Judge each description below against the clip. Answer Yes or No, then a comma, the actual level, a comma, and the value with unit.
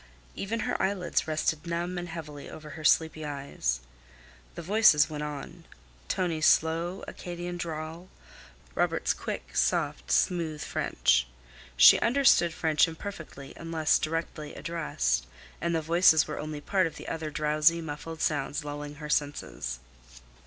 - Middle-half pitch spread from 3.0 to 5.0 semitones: No, narrow, 2.5 semitones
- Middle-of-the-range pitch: Yes, medium, 160 Hz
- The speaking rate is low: Yes, slow, 130 wpm